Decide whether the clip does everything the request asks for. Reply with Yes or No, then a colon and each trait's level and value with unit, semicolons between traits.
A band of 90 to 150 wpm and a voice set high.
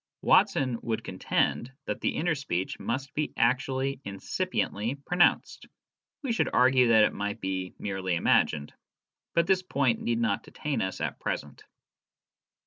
No: average, 140 wpm; low, 120 Hz